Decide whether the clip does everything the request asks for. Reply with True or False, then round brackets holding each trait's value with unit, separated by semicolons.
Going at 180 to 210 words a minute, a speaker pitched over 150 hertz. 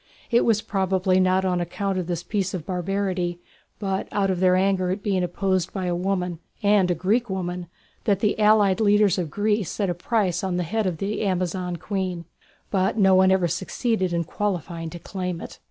True (200 wpm; 185 Hz)